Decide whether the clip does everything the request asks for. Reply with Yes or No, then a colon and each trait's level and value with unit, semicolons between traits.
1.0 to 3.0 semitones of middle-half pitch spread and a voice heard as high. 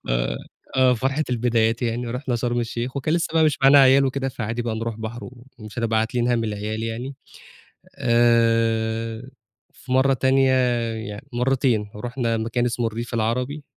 No: narrow, 2.4 semitones; low, 120 Hz